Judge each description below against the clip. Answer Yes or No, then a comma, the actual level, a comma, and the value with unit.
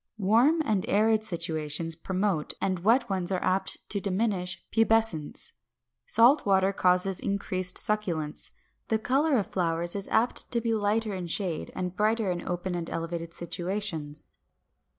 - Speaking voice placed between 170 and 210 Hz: Yes, high, 190 Hz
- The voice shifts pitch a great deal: No, average, 3.9 semitones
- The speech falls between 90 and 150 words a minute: Yes, average, 145 wpm